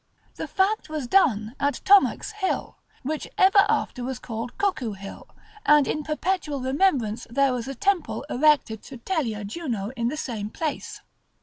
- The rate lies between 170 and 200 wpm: No, average, 160 wpm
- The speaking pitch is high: Yes, very high, 275 Hz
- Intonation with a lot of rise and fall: Yes, wide, 5.9 semitones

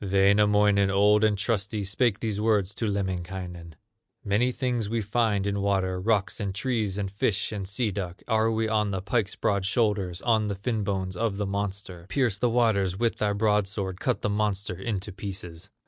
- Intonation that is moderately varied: No, narrow, 2.1 semitones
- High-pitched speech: No, low, 100 Hz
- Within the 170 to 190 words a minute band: Yes, average, 180 wpm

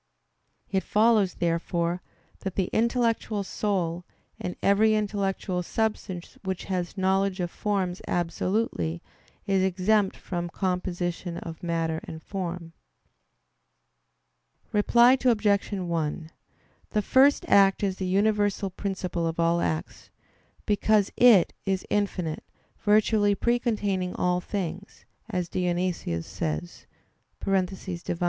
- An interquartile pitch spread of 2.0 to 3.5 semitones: Yes, average, 3.0 semitones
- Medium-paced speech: No, slow, 105 wpm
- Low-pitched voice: No, high, 190 Hz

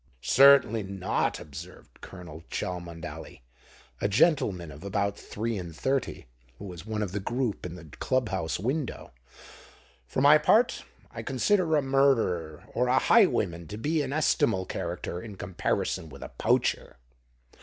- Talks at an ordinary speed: Yes, average, 145 wpm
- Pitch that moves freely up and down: Yes, wide, 7.1 semitones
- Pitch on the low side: Yes, low, 100 Hz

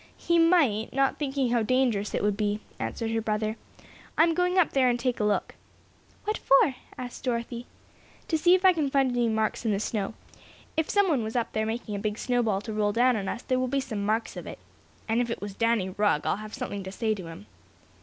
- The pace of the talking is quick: Yes, fast, 235 wpm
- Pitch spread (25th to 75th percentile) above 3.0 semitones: Yes, average, 4.1 semitones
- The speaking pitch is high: Yes, high, 235 Hz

